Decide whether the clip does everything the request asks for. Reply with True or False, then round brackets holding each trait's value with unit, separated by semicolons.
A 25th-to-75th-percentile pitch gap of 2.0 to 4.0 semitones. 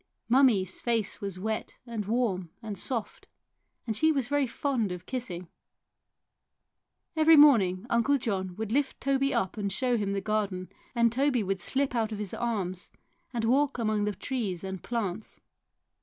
False (4.6 semitones)